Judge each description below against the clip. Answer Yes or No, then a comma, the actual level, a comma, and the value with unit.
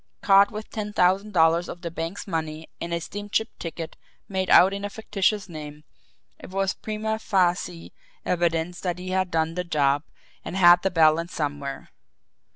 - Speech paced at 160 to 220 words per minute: Yes, average, 165 wpm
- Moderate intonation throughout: Yes, average, 3.2 semitones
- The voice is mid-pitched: Yes, medium, 180 Hz